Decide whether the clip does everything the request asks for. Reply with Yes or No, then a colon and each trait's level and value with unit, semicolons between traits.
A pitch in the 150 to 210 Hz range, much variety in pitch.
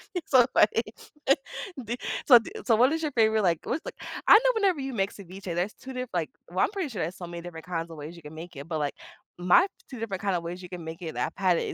Yes: medium, 185 Hz; wide, 6.2 semitones